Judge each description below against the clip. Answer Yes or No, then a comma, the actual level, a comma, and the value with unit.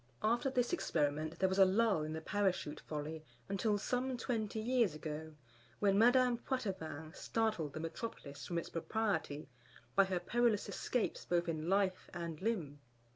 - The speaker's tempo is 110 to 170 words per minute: Yes, average, 155 wpm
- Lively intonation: Yes, wide, 6.2 semitones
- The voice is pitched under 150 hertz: No, high, 190 Hz